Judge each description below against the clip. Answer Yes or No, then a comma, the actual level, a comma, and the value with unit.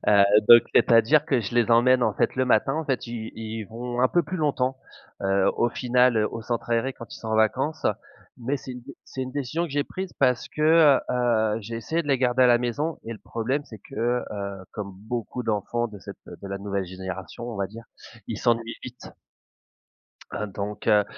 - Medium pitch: No, low, 120 Hz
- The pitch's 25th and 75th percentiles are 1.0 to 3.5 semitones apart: Yes, average, 3.2 semitones